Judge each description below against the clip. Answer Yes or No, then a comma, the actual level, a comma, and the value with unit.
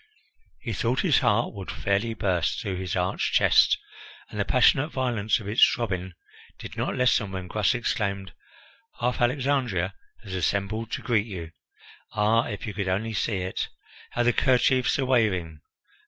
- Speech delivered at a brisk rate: No, average, 160 wpm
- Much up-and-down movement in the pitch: No, average, 4.1 semitones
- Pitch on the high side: No, low, 105 Hz